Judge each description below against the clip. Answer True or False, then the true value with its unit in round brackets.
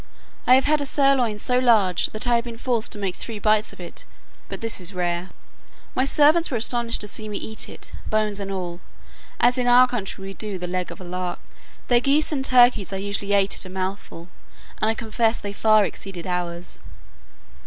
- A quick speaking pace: True (210 wpm)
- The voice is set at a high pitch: True (215 Hz)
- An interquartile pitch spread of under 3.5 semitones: False (4.3 semitones)